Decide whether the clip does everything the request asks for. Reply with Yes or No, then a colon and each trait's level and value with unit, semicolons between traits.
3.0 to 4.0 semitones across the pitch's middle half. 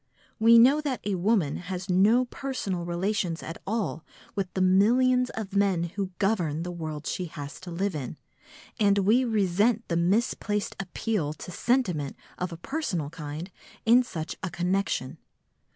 No: average, 4.5 semitones